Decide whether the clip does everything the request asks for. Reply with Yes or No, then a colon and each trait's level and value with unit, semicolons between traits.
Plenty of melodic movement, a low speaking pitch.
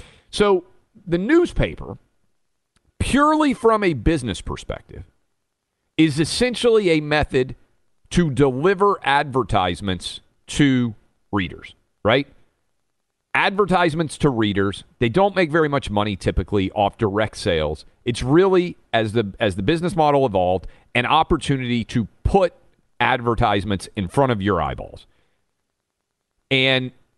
Yes: wide, 8.6 semitones; low, 130 Hz